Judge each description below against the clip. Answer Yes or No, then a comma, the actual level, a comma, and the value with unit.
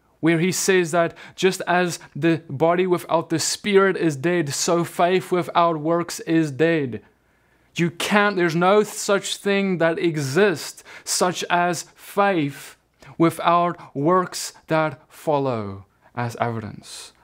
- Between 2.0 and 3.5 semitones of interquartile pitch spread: Yes, narrow, 2.6 semitones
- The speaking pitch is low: No, medium, 170 Hz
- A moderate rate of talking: No, slow, 125 wpm